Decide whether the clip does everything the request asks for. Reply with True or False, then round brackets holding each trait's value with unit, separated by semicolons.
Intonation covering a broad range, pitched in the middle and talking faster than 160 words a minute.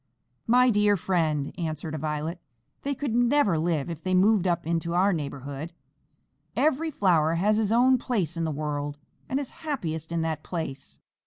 True (5.8 semitones; 170 Hz; 170 wpm)